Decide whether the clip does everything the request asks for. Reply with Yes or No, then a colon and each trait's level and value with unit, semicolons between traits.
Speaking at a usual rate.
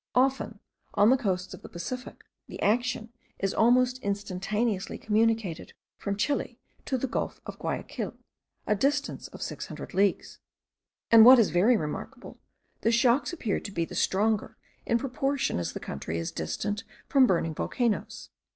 Yes: average, 155 wpm